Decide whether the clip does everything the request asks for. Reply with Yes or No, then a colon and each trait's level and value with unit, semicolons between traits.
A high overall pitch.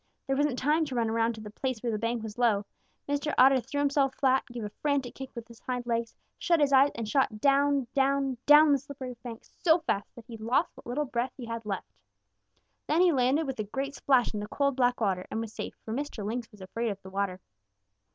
Yes: very high, 250 Hz